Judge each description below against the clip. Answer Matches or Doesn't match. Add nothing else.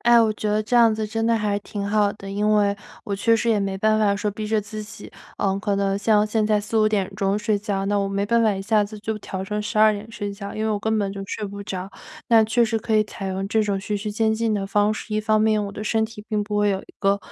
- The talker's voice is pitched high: Matches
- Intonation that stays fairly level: Matches